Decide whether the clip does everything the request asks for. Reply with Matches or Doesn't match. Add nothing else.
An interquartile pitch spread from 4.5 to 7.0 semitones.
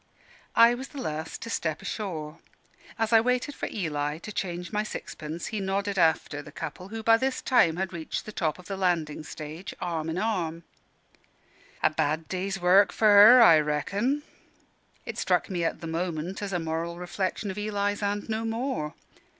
Matches